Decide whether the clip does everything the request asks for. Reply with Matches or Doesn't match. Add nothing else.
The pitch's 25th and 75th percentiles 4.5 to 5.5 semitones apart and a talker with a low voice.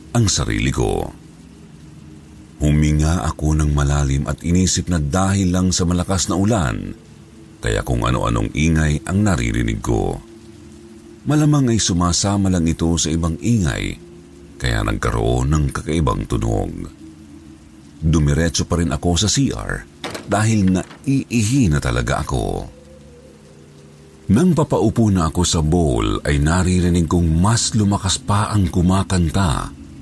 Matches